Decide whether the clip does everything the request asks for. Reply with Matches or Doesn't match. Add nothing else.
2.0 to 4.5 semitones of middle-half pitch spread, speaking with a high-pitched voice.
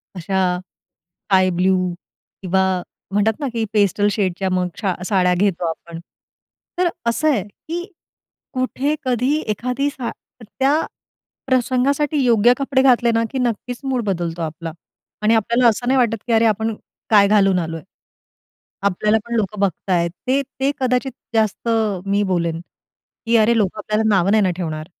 Doesn't match